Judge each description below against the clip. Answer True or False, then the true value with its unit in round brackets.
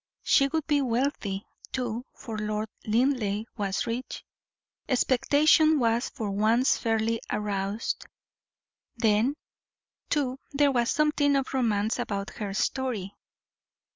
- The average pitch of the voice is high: True (235 Hz)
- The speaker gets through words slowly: True (110 wpm)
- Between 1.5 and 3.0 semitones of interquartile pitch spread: False (4.2 semitones)